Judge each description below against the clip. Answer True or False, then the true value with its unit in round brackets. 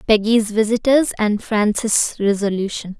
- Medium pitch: False (215 Hz)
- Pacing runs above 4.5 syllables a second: False (4.4 syllables/s)